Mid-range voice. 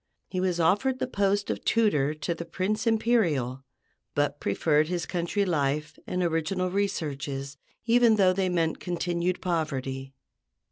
Yes: medium, 175 Hz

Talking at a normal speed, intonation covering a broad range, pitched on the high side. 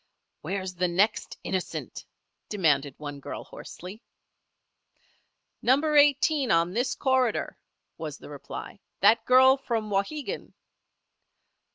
No: slow, 100 wpm; wide, 6.4 semitones; high, 215 Hz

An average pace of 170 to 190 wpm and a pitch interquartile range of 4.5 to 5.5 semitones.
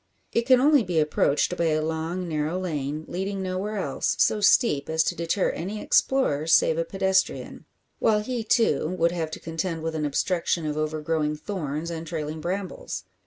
No: average, 175 wpm; average, 3.7 semitones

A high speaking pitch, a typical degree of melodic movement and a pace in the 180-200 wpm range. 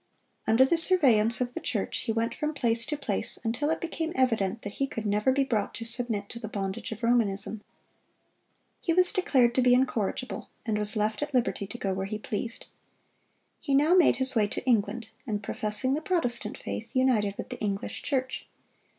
Yes: high, 235 Hz; average, 3.8 semitones; average, 195 wpm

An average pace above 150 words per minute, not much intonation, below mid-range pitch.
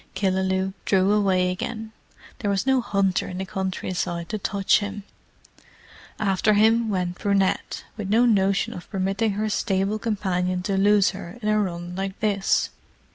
No: average, 160 wpm; narrow, 2.0 semitones; high, 195 Hz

